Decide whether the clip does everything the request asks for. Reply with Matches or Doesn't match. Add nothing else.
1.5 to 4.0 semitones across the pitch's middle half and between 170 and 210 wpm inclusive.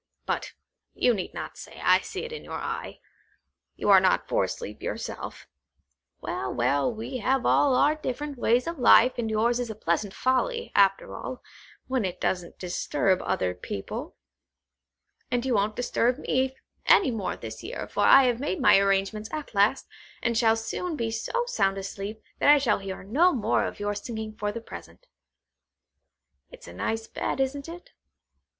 Doesn't match